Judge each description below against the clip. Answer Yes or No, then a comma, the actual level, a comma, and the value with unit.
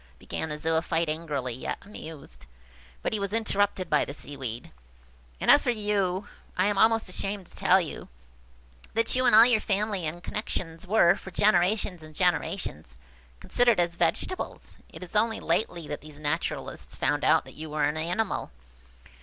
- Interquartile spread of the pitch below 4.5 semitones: No, wide, 5.4 semitones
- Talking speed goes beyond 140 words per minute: Yes, average, 160 wpm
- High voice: No, medium, 175 Hz